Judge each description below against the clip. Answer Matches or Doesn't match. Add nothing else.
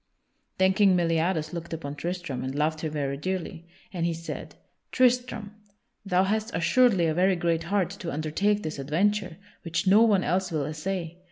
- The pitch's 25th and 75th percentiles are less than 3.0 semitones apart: Doesn't match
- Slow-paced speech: Doesn't match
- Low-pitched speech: Doesn't match